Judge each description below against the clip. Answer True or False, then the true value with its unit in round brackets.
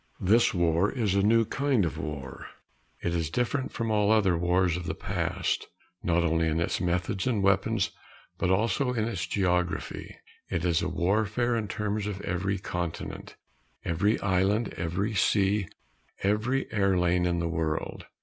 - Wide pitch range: False (3.6 semitones)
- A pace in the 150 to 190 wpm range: True (160 wpm)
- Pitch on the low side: True (95 Hz)